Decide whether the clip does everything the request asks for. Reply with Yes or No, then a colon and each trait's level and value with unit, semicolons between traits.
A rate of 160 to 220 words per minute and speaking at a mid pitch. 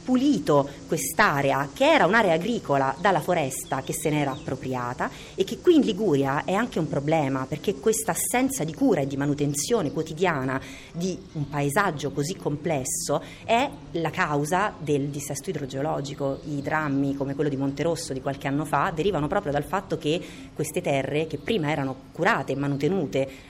Yes: average, 165 wpm; medium, 150 Hz